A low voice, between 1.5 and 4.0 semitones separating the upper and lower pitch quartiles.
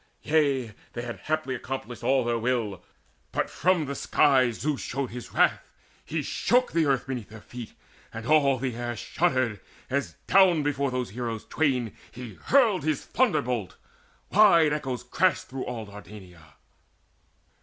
No: low, 130 Hz; average, 4.4 semitones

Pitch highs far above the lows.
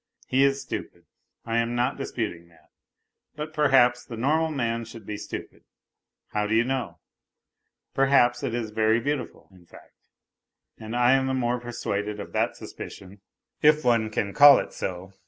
No: average, 3.7 semitones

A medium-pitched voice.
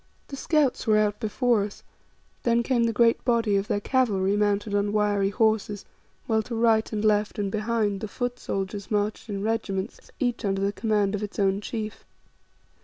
No: high, 210 Hz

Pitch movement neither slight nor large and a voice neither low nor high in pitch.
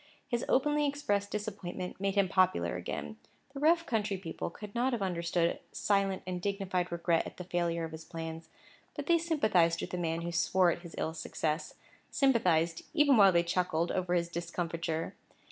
Yes: average, 3.6 semitones; medium, 180 Hz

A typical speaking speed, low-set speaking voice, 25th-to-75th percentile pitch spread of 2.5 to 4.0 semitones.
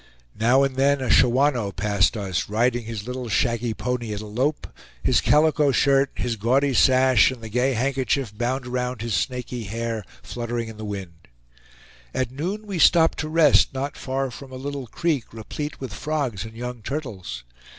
Yes: average, 175 wpm; low, 125 Hz; average, 3.4 semitones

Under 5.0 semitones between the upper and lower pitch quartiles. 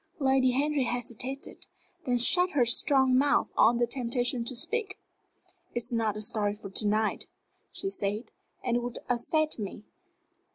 Yes: average, 2.9 semitones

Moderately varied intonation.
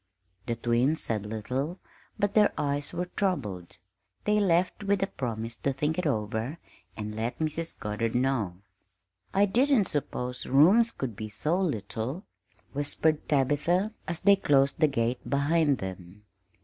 No: wide, 7.3 semitones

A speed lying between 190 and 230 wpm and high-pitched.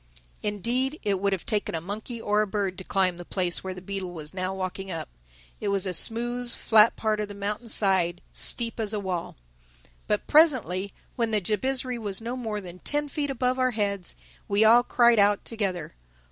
Yes: average, 200 wpm; high, 205 Hz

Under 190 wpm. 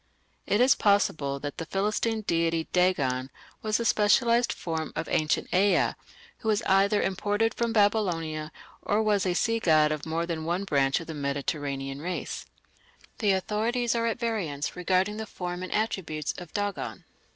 Yes: average, 165 wpm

